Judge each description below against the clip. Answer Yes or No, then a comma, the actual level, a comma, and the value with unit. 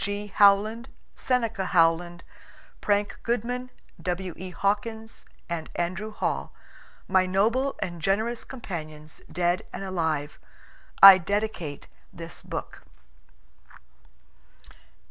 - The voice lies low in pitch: No, high, 195 Hz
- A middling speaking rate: No, slow, 95 wpm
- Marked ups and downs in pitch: No, average, 4.0 semitones